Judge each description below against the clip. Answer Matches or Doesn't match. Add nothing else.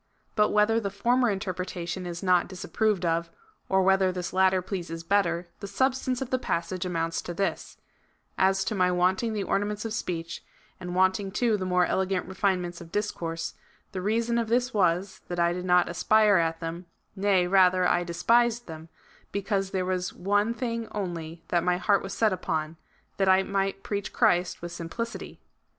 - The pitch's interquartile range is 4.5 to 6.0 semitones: Doesn't match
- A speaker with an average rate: Matches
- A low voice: Doesn't match